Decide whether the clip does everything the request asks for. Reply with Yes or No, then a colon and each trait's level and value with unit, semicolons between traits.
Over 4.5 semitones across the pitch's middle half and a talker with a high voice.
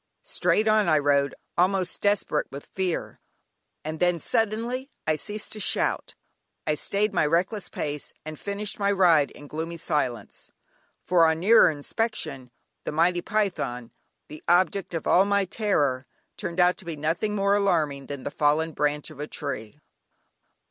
No: average, 5.2 semitones; medium, 170 Hz